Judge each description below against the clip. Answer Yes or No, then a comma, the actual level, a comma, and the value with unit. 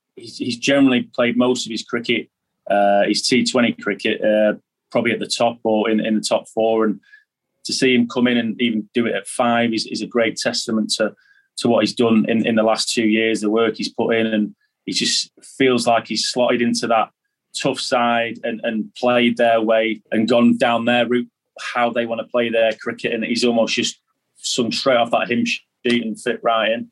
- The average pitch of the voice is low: Yes, low, 115 Hz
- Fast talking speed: Yes, fast, 220 wpm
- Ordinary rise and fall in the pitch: No, narrow, 1.6 semitones